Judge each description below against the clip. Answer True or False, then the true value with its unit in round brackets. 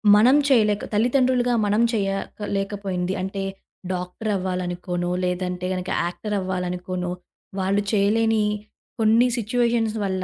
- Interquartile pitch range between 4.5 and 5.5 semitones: False (3.4 semitones)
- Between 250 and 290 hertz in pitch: False (200 Hz)